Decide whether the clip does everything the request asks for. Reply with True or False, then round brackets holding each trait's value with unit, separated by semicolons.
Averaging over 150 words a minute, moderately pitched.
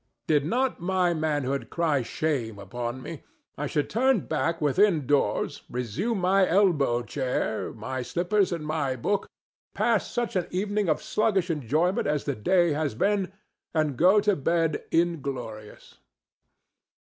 False (140 wpm; 160 Hz)